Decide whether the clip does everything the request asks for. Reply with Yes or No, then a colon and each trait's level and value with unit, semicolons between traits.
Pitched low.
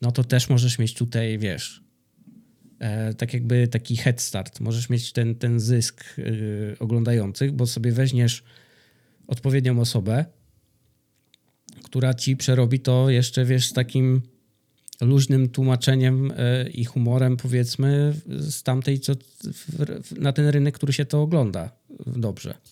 Yes: low, 125 Hz